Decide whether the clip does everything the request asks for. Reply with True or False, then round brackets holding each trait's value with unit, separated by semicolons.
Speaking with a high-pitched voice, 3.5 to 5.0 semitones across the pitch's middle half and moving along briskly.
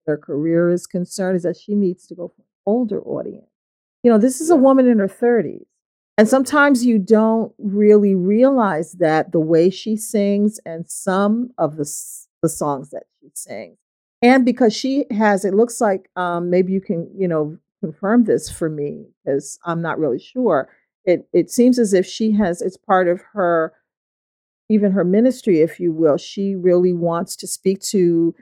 False (195 Hz; 4.5 semitones; 185 wpm)